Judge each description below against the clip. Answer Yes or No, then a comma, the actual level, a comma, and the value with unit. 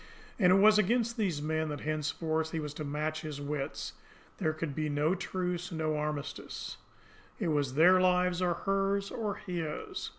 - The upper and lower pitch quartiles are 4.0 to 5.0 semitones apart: No, average, 3.5 semitones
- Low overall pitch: No, medium, 160 Hz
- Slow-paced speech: No, average, 170 wpm